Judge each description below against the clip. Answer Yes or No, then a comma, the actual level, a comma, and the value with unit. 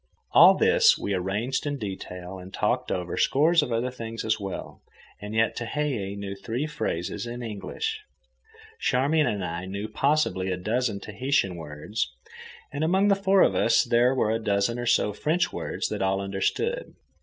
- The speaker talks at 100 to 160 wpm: No, average, 170 wpm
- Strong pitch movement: Yes, wide, 6.1 semitones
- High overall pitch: No, low, 115 Hz